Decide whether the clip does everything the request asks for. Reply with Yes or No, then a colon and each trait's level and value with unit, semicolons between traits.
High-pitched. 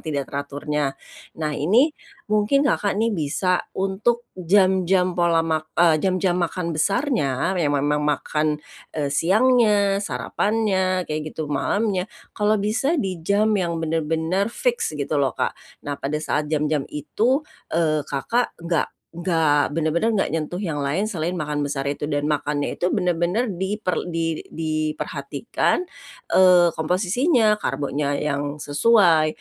No: medium, 170 Hz